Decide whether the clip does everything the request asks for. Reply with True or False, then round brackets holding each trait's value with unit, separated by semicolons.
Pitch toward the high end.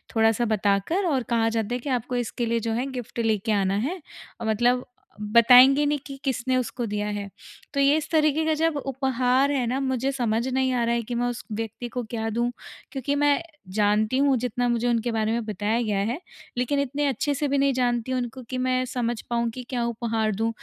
True (245 Hz)